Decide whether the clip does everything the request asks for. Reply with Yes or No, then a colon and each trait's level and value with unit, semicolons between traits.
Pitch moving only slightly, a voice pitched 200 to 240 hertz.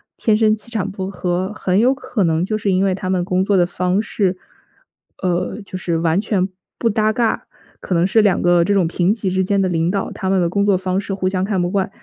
No: narrow, 2.1 semitones; high, 190 Hz